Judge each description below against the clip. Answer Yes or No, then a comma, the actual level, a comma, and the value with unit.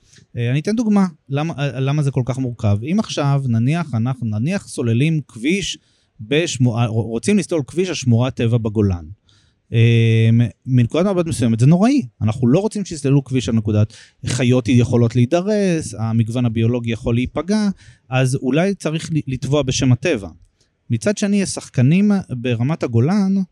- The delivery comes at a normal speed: Yes, average, 140 wpm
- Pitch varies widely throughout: Yes, wide, 5.8 semitones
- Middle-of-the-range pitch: No, low, 130 Hz